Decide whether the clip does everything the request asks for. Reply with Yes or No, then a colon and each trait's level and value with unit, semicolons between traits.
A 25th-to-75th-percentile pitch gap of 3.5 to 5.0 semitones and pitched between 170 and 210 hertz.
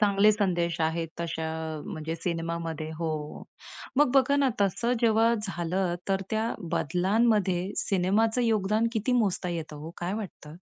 Yes: average, 4.7 semitones; high, 190 Hz